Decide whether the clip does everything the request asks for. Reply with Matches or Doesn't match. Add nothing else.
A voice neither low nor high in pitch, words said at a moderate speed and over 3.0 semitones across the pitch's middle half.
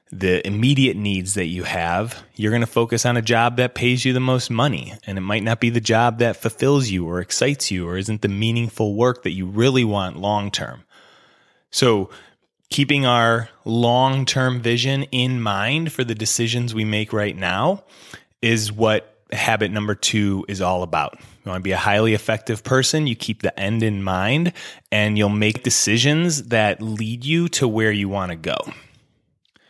Doesn't match